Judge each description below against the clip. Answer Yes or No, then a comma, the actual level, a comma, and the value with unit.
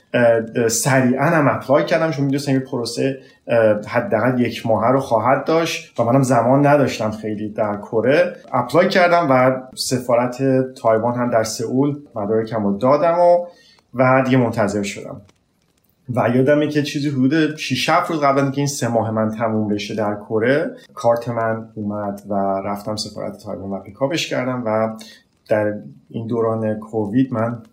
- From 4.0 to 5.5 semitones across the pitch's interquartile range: No, average, 3.6 semitones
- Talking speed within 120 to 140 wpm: No, average, 150 wpm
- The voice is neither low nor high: No, low, 120 Hz